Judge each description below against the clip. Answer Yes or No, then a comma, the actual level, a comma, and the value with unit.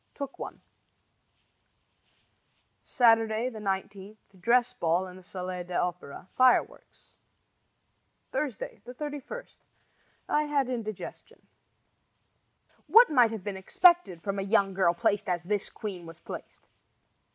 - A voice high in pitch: Yes, high, 210 Hz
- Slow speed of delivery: Yes, slow, 110 wpm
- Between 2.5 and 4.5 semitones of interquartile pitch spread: No, average, 5.3 semitones